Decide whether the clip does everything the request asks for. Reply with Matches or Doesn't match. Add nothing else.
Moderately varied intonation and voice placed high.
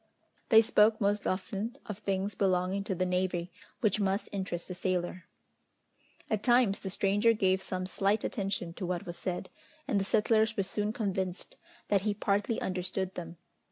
Doesn't match